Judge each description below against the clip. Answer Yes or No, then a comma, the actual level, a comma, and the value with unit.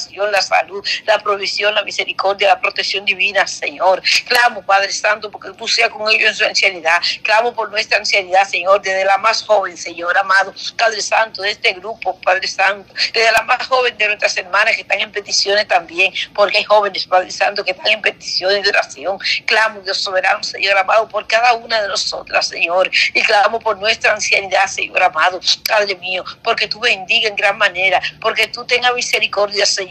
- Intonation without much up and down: Yes, narrow, 2.3 semitones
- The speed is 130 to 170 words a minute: No, fast, 190 wpm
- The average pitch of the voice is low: No, high, 205 Hz